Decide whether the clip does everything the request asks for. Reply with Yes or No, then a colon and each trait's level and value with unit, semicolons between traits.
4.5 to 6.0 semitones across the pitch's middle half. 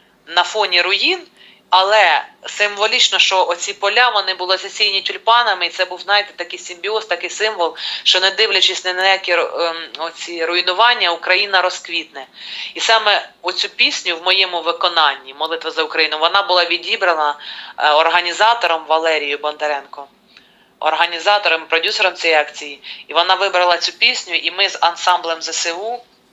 No: average, 3.1 semitones